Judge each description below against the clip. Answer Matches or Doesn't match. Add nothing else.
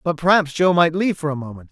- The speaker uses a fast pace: Matches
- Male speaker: Matches